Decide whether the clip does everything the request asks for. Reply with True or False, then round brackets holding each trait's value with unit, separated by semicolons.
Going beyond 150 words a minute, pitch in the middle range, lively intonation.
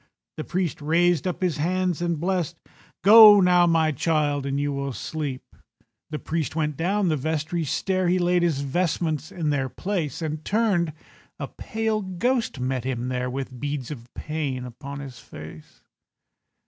False (160 wpm; 155 Hz; 4.3 semitones)